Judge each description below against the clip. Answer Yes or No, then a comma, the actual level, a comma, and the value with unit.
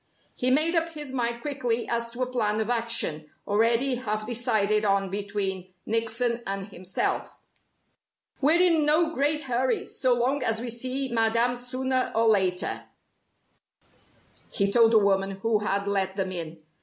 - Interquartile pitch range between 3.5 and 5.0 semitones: Yes, average, 4.2 semitones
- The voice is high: Yes, high, 230 Hz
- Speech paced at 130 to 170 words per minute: Yes, average, 155 wpm